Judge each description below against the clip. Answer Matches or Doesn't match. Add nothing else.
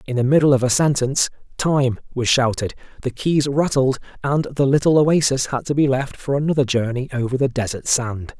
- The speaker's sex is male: Matches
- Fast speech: Doesn't match